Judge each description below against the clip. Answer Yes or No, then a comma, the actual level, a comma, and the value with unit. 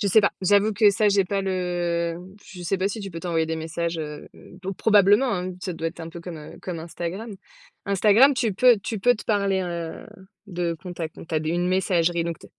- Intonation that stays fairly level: No, average, 3.1 semitones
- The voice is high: No, medium, 180 Hz